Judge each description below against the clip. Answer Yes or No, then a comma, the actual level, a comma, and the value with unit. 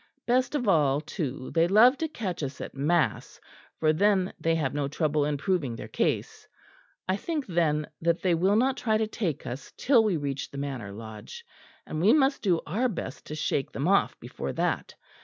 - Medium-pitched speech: Yes, medium, 170 Hz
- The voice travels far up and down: Yes, wide, 6.9 semitones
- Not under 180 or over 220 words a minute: Yes, average, 195 wpm